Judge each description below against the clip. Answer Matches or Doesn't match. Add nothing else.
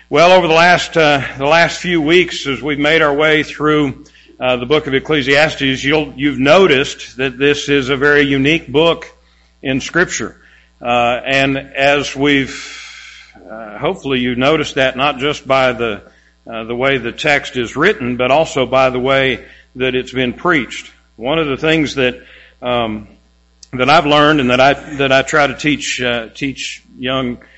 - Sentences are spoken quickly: Doesn't match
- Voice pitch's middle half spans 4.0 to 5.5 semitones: Doesn't match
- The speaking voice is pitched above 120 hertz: Matches